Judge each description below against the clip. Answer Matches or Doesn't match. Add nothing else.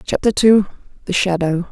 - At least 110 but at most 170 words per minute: Matches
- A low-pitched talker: Doesn't match